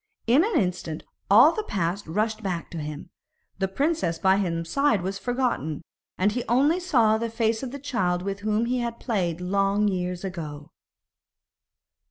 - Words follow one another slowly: No, average, 170 wpm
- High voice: Yes, high, 205 Hz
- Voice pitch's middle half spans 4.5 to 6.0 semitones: Yes, average, 5.1 semitones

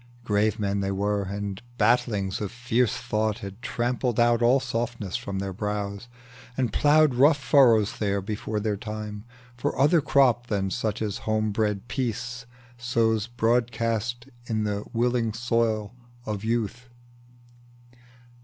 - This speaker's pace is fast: No, slow, 135 wpm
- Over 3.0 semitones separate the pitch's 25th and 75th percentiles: No, average, 2.7 semitones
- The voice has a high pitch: No, low, 110 Hz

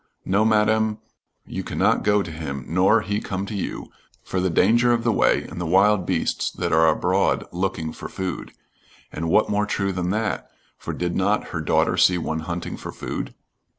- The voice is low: Yes, very low, 95 Hz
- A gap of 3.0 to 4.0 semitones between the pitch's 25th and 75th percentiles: Yes, average, 3.7 semitones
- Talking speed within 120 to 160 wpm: No, average, 190 wpm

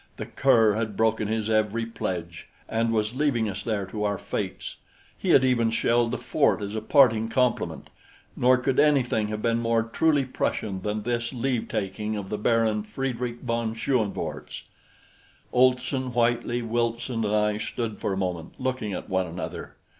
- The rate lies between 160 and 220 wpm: Yes, average, 170 wpm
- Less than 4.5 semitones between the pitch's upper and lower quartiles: Yes, narrow, 2.4 semitones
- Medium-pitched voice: No, low, 115 Hz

